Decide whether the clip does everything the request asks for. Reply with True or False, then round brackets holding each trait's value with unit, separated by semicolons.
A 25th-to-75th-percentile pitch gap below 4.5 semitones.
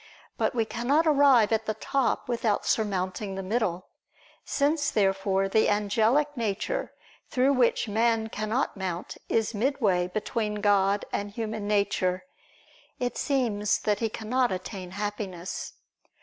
True (3.3 semitones)